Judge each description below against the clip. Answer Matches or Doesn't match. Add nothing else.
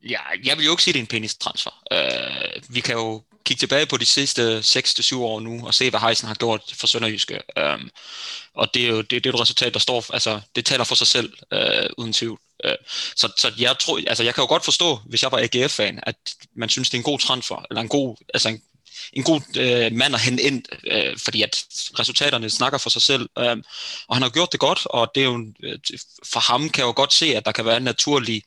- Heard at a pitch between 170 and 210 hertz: Doesn't match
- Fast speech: Matches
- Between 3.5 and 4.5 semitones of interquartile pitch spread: Doesn't match